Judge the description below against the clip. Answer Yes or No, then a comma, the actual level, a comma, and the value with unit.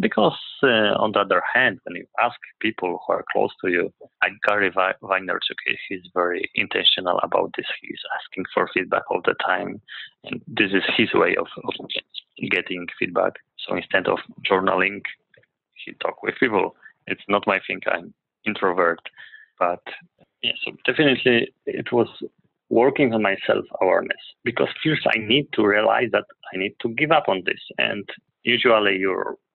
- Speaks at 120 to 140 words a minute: No, average, 160 wpm